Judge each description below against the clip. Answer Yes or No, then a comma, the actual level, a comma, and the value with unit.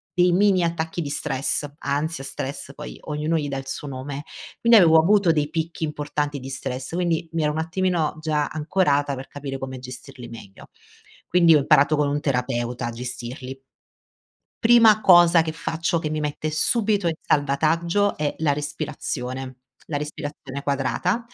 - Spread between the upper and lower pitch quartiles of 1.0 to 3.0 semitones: No, average, 3.5 semitones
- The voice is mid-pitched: Yes, medium, 150 Hz